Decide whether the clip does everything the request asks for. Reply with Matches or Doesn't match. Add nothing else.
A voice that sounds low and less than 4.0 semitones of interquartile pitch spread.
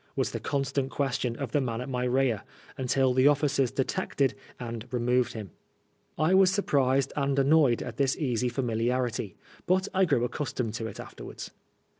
Matches